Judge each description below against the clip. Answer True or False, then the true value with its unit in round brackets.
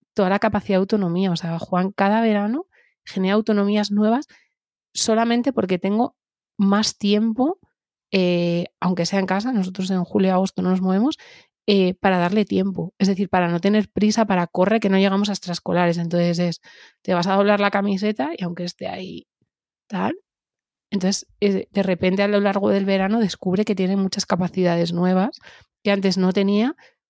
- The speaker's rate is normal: True (170 wpm)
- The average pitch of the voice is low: False (195 Hz)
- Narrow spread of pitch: True (2.3 semitones)